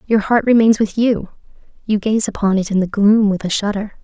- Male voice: No, female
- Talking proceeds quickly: Yes, fast, 225 wpm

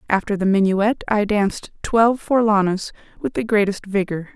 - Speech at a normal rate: Yes, average, 150 wpm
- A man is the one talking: No, female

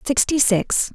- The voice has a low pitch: No, very high, 250 Hz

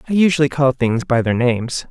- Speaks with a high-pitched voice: No, low, 135 Hz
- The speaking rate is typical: No, fast, 220 wpm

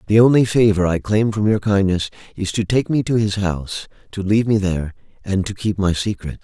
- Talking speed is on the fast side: Yes, fast, 225 wpm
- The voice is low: Yes, low, 100 Hz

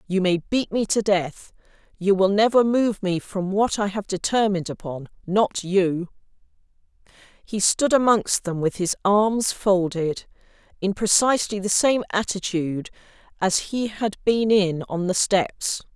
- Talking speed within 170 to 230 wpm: No, average, 145 wpm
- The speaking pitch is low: No, high, 200 Hz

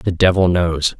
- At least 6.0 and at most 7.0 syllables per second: No, 4.2 syllables/s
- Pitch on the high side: No, very low, 90 Hz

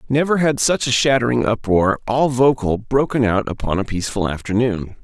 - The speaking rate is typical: Yes, average, 165 wpm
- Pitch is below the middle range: Yes, low, 120 Hz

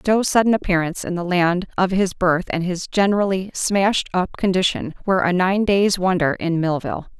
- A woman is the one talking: Yes, female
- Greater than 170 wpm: Yes, average, 185 wpm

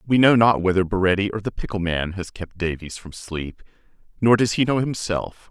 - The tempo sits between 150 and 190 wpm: No, fast, 205 wpm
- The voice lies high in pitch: No, low, 100 Hz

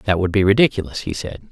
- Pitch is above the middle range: No, low, 100 Hz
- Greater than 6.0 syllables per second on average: Yes, 6.5 syllables/s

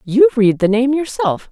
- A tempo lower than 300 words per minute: Yes, average, 200 wpm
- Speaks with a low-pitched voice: No, high, 245 Hz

